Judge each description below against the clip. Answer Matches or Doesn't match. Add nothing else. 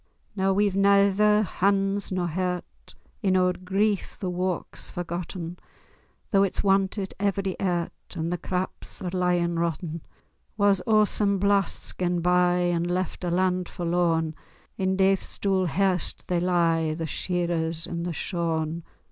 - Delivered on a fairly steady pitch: Matches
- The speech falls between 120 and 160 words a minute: Matches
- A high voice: Doesn't match